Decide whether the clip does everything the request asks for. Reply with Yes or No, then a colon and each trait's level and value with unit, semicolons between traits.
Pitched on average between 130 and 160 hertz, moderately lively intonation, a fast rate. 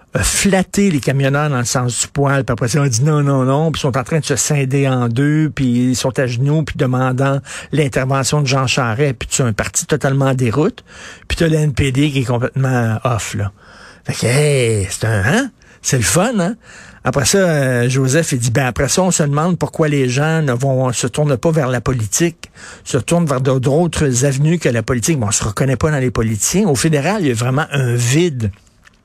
Yes: low, 135 Hz; average, 3.2 semitones; fast, 225 wpm